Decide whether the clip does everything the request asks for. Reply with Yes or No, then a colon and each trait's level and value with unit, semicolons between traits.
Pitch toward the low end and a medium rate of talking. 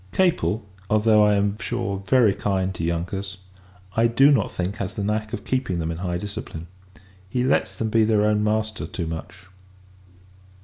Yes: low, 105 Hz; average, 175 wpm